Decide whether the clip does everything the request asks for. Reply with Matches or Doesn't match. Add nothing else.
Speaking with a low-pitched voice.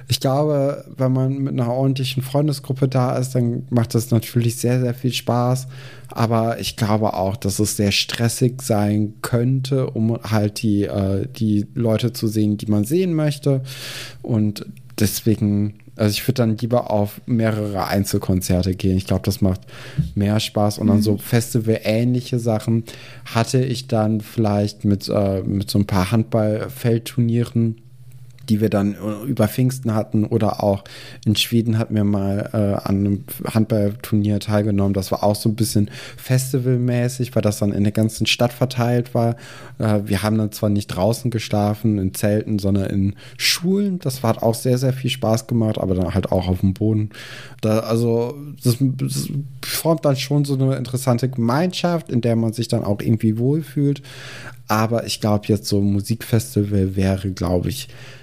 Matches